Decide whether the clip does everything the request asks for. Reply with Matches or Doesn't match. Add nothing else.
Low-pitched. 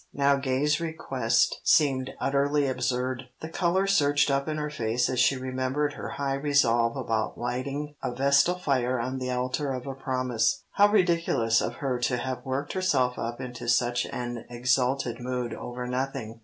Matches